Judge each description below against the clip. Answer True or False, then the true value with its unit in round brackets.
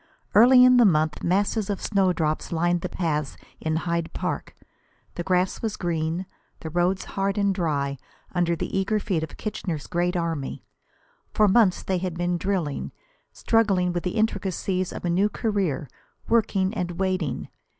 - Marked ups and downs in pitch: False (2.9 semitones)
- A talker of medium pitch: True (180 Hz)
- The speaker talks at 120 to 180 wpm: True (160 wpm)